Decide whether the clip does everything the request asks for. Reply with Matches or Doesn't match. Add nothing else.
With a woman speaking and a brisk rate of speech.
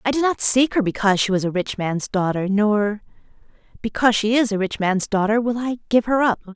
Matches